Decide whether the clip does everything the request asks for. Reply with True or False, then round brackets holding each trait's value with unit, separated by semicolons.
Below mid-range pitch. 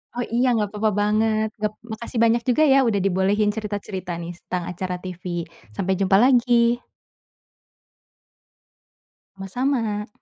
False (210 Hz)